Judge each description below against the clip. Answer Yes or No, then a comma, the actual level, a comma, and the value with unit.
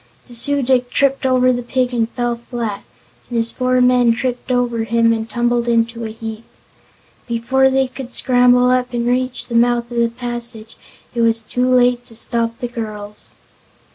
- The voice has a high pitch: Yes, high, 240 Hz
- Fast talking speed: No, average, 185 wpm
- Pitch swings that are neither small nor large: No, narrow, 1.5 semitones